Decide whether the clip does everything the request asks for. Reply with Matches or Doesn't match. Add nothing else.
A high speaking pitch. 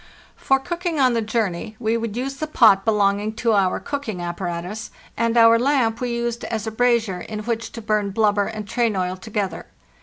Matches